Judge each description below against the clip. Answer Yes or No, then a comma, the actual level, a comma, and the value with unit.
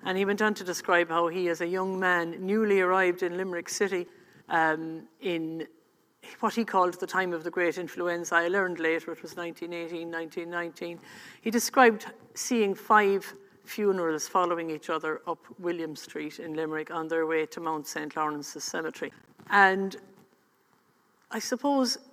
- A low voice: No, medium, 175 Hz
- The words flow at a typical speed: Yes, average, 160 wpm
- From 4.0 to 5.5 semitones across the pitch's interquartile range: No, average, 3.1 semitones